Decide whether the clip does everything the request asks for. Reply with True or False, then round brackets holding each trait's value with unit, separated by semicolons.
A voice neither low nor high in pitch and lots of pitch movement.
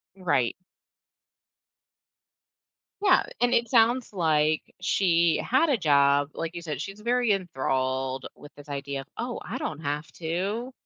True (165 Hz; 7.3 semitones)